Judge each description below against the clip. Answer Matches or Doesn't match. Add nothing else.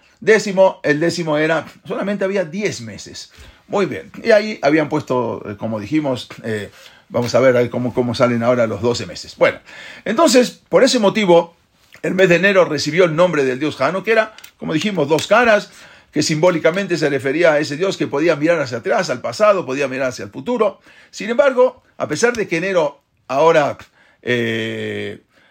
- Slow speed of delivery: Doesn't match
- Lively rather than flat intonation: Matches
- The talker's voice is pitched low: Doesn't match